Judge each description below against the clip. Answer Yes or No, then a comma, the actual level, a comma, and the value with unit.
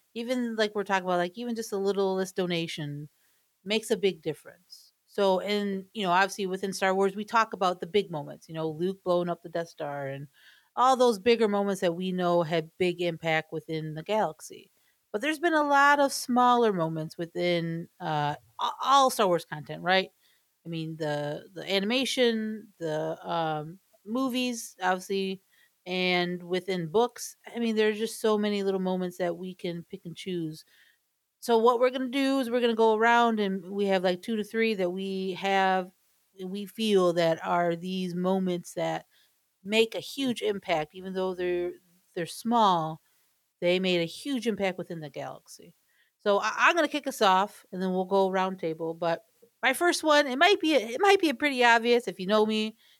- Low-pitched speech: No, high, 190 Hz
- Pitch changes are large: No, average, 4.5 semitones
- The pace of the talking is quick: No, average, 190 wpm